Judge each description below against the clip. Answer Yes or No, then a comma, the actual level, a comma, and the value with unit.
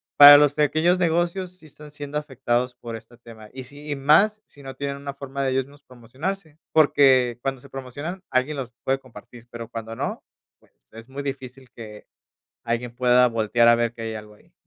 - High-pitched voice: No, low, 135 Hz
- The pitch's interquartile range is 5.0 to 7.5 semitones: No, average, 3.4 semitones